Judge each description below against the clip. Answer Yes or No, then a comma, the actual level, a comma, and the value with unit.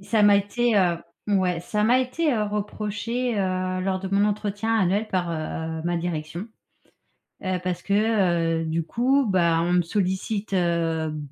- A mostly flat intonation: No, average, 3.4 semitones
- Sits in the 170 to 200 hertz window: Yes, high, 190 Hz